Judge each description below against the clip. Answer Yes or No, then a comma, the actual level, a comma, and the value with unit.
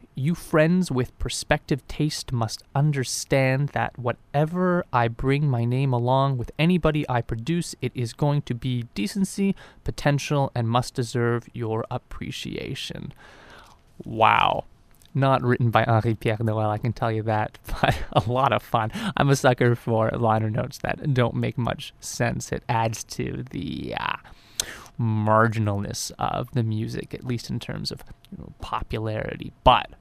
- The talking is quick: No, average, 150 wpm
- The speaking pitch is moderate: No, low, 125 Hz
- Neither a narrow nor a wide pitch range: Yes, average, 3.7 semitones